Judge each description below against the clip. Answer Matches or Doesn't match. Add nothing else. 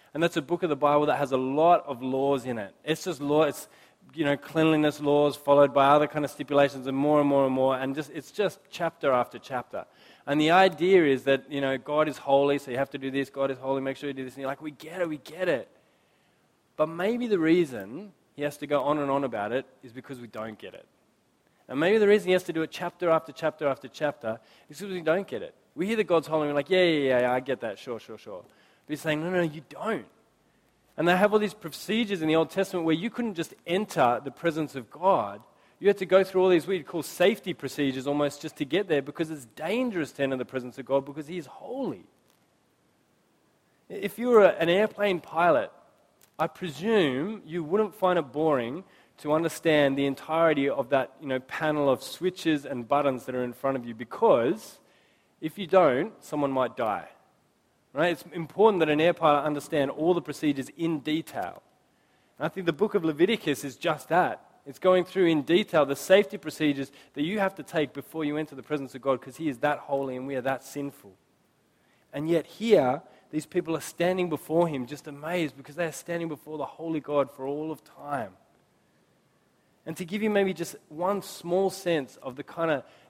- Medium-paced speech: Doesn't match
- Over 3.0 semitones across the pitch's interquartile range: Matches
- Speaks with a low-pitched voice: Doesn't match